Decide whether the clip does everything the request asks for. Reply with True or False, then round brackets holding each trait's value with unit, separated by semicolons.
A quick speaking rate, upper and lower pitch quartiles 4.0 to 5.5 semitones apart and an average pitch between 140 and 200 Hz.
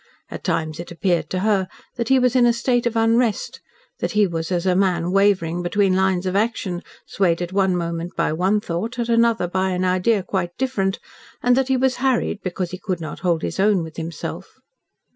True (210 wpm; 4.6 semitones; 190 Hz)